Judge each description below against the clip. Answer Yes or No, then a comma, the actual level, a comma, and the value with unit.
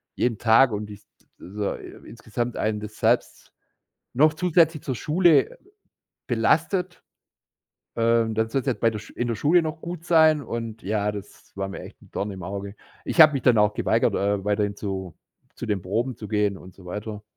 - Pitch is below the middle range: Yes, low, 110 Hz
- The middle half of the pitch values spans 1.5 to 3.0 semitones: No, average, 4.9 semitones